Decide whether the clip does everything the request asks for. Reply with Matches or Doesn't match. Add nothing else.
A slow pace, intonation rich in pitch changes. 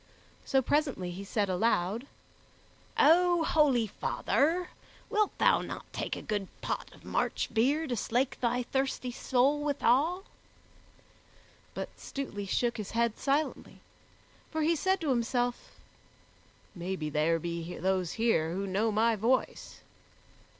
Matches